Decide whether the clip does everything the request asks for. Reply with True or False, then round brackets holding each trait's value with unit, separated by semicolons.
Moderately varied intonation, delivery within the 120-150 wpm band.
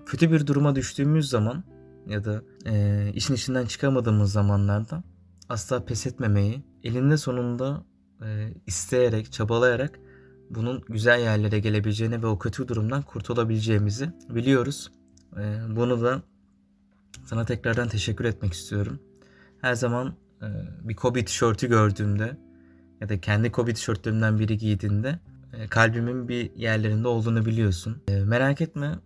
True (3.3 semitones; 125 wpm)